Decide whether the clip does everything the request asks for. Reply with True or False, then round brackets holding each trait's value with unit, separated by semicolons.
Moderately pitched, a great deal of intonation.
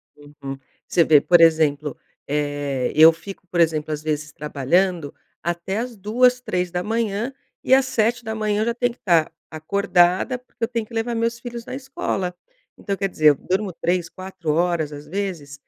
True (180 Hz; 6.3 semitones)